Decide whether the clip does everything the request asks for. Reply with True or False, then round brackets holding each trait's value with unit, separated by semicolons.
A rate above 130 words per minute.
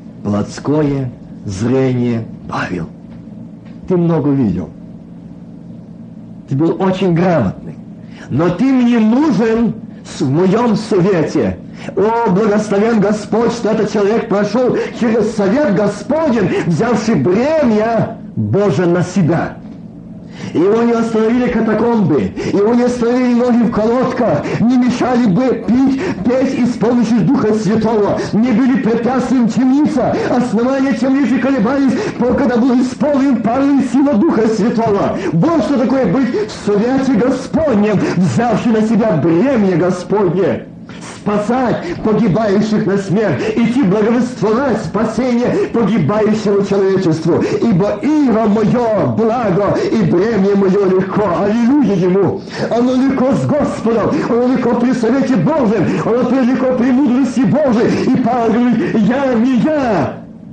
False (115 wpm)